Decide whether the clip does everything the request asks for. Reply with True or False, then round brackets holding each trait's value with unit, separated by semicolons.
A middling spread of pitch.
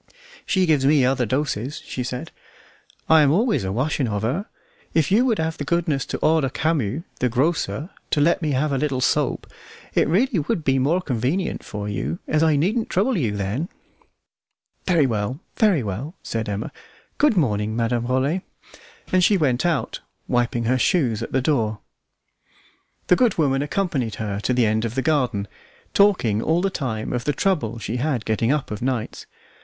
False (5.9 semitones)